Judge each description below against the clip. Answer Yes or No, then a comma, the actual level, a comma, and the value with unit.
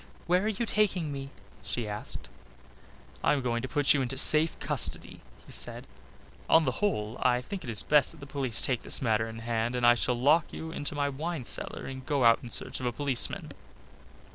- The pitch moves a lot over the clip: No, average, 4.3 semitones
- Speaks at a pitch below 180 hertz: Yes, low, 135 Hz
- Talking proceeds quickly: Yes, fast, 215 wpm